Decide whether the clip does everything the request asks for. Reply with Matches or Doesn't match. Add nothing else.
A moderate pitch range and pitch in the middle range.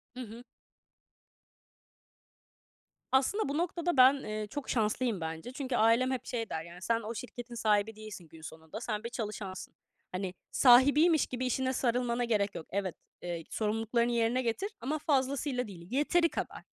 Doesn't match